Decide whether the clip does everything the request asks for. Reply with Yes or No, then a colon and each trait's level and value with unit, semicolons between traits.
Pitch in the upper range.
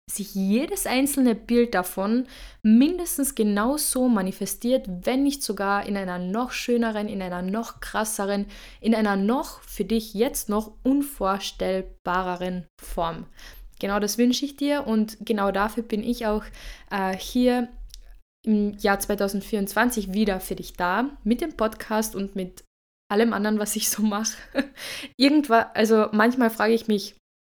Yes: high, 215 Hz